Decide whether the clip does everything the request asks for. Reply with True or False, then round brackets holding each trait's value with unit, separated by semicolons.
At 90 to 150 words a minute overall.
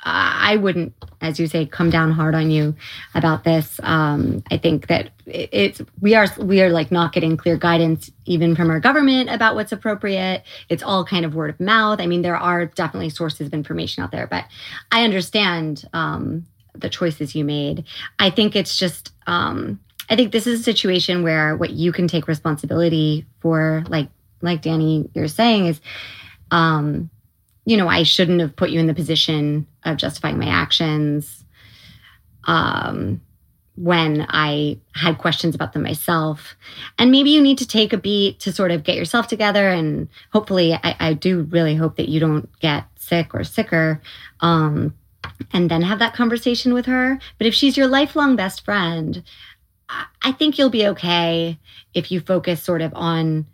False (180 wpm)